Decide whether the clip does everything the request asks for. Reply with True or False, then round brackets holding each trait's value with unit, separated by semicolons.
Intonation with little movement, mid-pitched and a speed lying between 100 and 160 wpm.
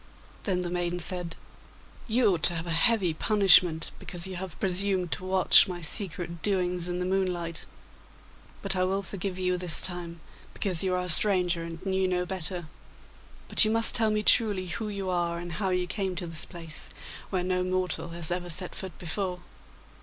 False (1.7 semitones; 180 Hz; 190 wpm)